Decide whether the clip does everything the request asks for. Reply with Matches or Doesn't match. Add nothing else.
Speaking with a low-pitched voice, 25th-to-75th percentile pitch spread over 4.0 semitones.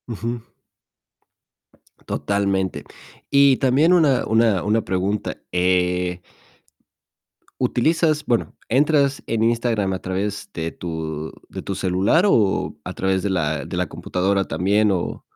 Matches